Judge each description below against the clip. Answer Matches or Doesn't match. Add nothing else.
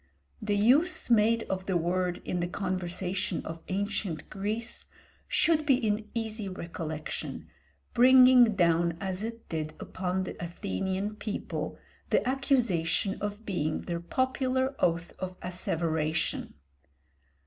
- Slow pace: Matches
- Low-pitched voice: Doesn't match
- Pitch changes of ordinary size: Matches